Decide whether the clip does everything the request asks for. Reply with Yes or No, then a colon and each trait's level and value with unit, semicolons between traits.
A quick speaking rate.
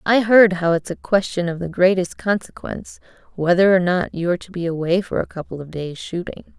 Yes: fast, 210 wpm